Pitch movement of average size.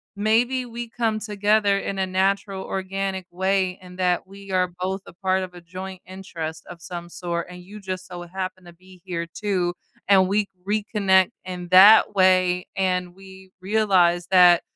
No: narrow, 1.6 semitones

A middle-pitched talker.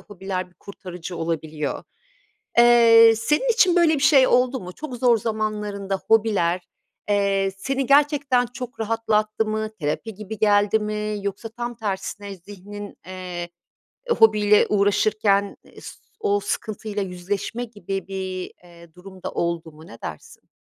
No: high, 205 Hz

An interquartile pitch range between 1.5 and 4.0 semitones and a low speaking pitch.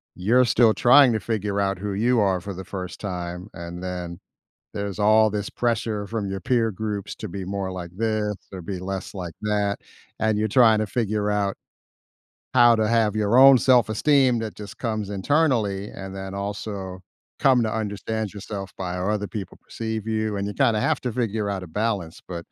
Yes: narrow, 2.5 semitones; low, 105 Hz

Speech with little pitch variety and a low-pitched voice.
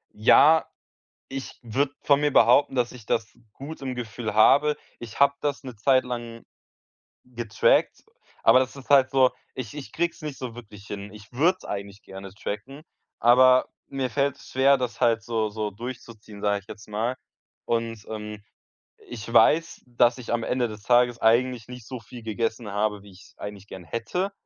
No: average, 3.5 semitones; low, 120 Hz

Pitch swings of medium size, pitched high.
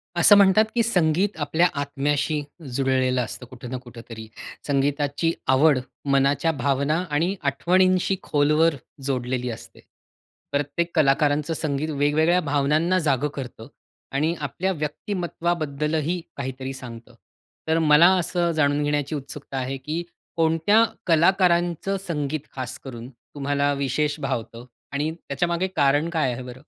No: average, 3.4 semitones; medium, 145 Hz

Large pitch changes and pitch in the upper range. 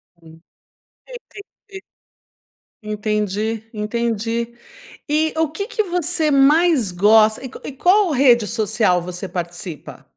Yes: wide, 6.7 semitones; high, 230 Hz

